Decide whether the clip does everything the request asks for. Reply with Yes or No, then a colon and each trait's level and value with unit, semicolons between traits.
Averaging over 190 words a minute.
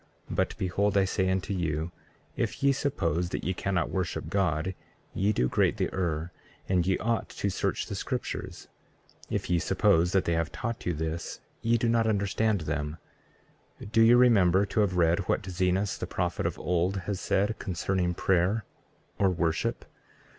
No: average, 170 wpm